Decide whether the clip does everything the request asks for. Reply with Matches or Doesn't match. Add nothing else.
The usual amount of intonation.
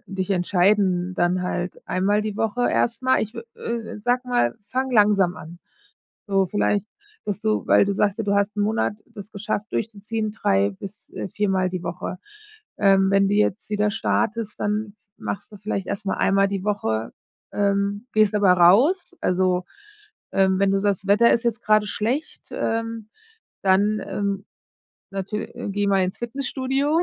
Doesn't match